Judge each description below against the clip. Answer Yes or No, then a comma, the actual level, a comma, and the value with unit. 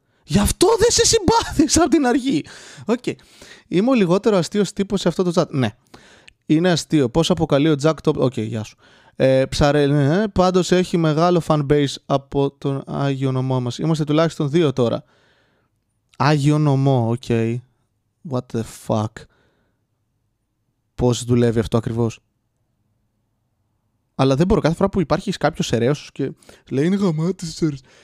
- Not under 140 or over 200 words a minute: Yes, average, 150 wpm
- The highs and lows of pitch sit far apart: Yes, wide, 6.8 semitones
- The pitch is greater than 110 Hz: Yes, medium, 140 Hz